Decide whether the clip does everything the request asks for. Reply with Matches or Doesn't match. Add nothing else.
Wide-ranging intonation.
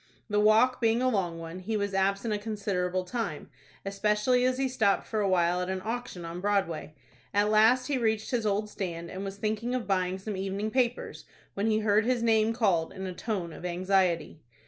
Doesn't match